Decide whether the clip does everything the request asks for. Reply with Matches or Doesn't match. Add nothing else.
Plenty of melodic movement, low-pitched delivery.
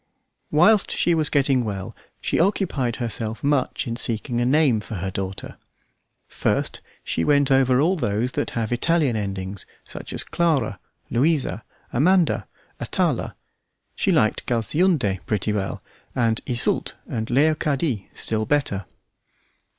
Matches